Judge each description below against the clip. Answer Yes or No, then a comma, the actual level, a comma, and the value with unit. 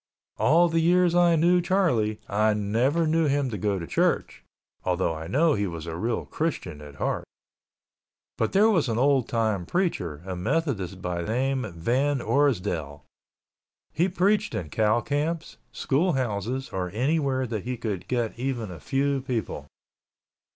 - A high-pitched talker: No, low, 125 Hz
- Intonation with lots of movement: Yes, wide, 7.8 semitones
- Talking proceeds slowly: No, average, 160 wpm